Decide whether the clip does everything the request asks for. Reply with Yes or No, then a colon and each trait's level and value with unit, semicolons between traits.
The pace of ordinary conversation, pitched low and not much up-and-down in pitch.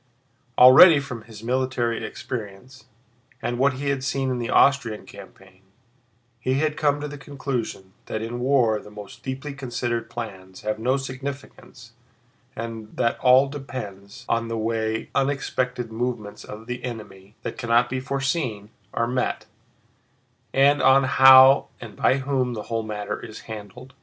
No: average, 145 wpm; low, 125 Hz; average, 3.3 semitones